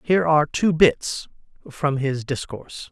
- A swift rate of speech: No, average, 145 wpm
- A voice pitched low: No, medium, 150 Hz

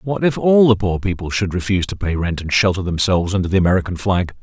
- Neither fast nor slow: No, fast, 245 wpm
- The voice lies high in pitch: No, very low, 95 Hz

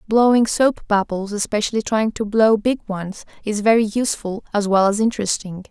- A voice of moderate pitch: No, high, 210 Hz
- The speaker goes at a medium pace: Yes, average, 170 wpm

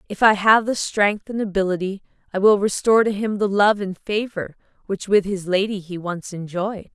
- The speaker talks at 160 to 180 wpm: No, average, 200 wpm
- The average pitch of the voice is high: Yes, high, 200 Hz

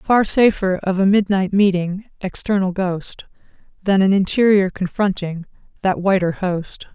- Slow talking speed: Yes, slow, 130 wpm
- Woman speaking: Yes, female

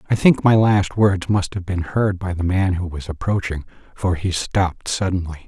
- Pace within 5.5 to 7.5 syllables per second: No, 4.9 syllables/s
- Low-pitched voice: Yes, very low, 95 Hz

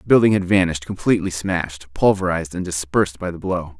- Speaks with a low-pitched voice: Yes, very low, 90 Hz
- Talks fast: No, average, 190 wpm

